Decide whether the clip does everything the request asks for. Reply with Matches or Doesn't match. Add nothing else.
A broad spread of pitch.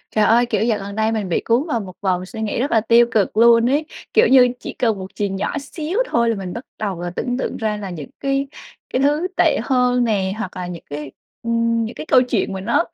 Doesn't match